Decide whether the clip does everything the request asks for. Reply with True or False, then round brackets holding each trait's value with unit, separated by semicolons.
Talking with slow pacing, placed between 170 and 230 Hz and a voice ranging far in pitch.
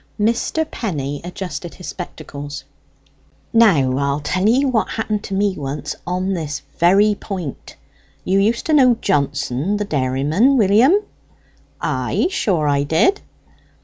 True (130 wpm; 185 Hz; 7.2 semitones)